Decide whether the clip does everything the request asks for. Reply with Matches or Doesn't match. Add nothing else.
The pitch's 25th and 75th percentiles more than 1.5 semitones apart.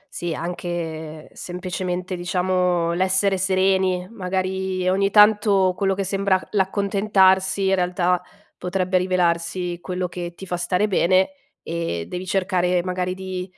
Doesn't match